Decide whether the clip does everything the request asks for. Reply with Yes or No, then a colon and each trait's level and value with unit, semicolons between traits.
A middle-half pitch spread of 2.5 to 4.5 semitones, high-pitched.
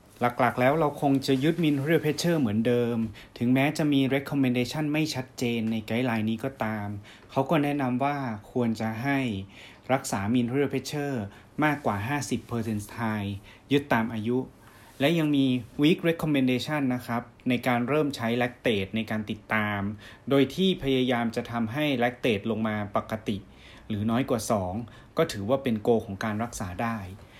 No: average, 3.7 semitones; low, 120 Hz